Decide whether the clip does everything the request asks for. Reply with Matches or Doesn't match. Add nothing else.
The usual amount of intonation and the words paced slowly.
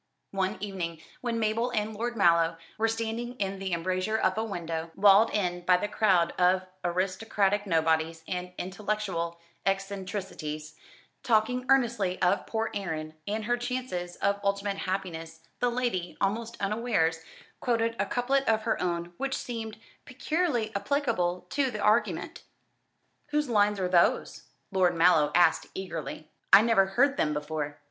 Doesn't match